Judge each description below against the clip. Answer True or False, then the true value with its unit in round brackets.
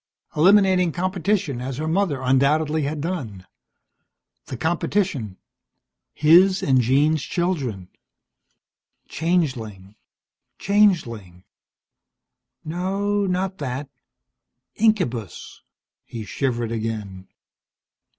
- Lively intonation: True (7.4 semitones)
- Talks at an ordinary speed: False (75 wpm)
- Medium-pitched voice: True (150 Hz)